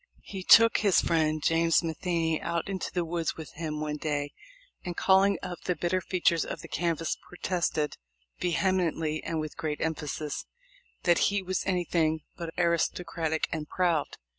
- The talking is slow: No, average, 155 wpm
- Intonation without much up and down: Yes, narrow, 2.3 semitones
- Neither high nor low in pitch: Yes, medium, 165 Hz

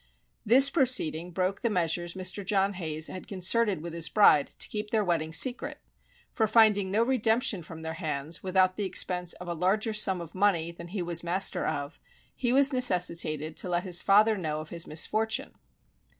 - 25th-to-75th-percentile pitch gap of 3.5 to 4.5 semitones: Yes, average, 4.0 semitones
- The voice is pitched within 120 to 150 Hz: No, medium, 185 Hz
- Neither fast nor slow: Yes, average, 185 wpm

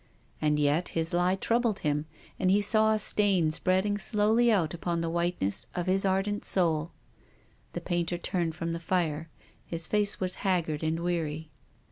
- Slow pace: No, average, 165 wpm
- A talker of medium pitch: Yes, medium, 175 Hz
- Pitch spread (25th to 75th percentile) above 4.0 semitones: No, average, 3.2 semitones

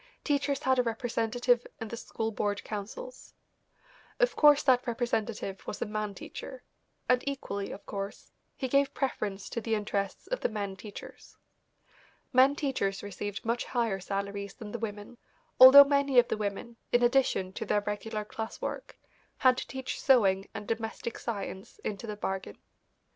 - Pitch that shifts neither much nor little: Yes, average, 4.0 semitones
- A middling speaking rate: Yes, average, 160 wpm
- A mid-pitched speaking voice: No, high, 225 Hz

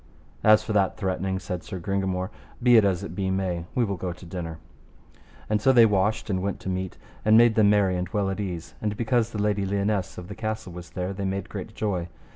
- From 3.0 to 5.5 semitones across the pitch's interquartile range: No, narrow, 2.5 semitones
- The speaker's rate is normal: No, fast, 235 wpm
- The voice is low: Yes, very low, 95 Hz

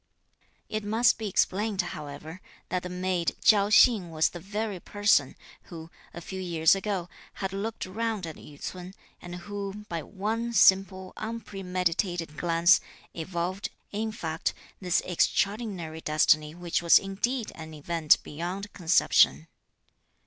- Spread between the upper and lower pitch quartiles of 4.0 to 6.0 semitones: No, average, 3.6 semitones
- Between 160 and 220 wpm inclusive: No, slow, 135 wpm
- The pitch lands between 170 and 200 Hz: Yes, medium, 185 Hz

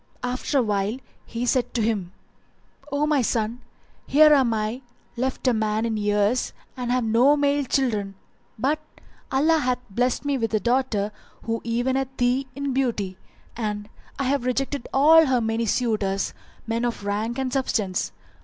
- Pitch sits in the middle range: No, high, 245 Hz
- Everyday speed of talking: Yes, average, 160 wpm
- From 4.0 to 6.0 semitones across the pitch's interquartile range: No, average, 3.6 semitones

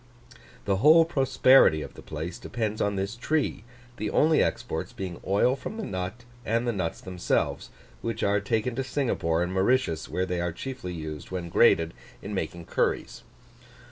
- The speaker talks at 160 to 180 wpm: Yes, average, 170 wpm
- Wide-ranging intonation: Yes, wide, 6.0 semitones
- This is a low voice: Yes, low, 100 Hz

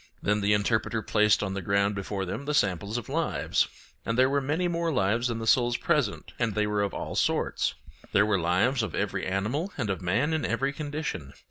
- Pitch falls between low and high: No, low, 110 Hz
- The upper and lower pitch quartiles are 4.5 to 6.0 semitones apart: Yes, average, 5.2 semitones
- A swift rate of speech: Yes, fast, 215 wpm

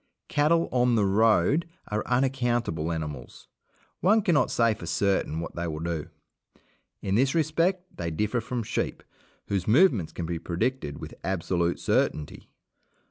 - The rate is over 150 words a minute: No, average, 140 wpm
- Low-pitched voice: Yes, low, 110 Hz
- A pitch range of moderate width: No, wide, 7.7 semitones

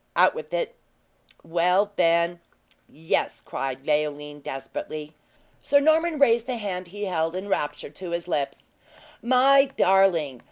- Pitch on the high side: No, medium, 180 Hz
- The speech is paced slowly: Yes, slow, 130 wpm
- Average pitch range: No, wide, 7.6 semitones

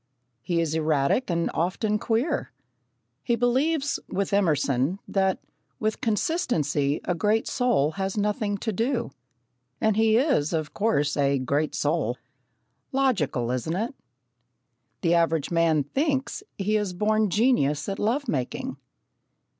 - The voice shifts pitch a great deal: Yes, wide, 6.7 semitones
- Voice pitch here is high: Yes, high, 195 Hz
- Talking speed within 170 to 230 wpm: No, slow, 135 wpm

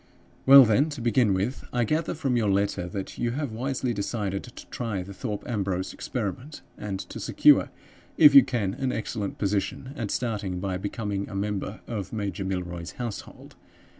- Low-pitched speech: Yes, low, 105 Hz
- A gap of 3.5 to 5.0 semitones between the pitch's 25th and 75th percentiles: Yes, average, 4.0 semitones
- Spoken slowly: No, average, 170 wpm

